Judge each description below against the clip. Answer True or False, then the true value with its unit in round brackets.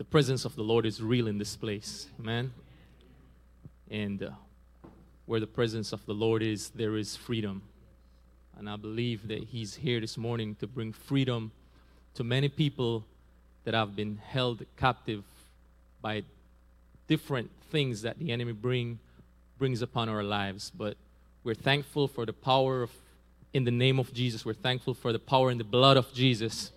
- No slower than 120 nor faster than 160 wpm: False (170 wpm)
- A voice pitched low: True (110 Hz)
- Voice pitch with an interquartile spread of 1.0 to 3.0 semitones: False (3.9 semitones)